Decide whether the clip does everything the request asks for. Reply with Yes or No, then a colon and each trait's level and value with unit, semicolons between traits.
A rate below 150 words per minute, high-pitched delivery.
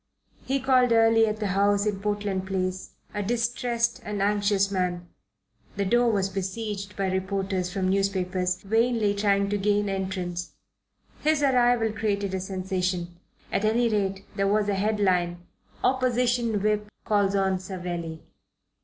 Yes: average, 140 wpm; high, 200 Hz